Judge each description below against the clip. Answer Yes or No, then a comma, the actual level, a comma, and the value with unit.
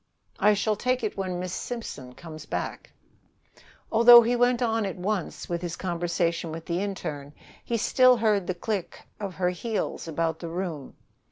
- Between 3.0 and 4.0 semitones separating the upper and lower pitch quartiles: No, average, 4.7 semitones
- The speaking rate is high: No, average, 170 wpm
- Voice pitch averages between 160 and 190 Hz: Yes, medium, 185 Hz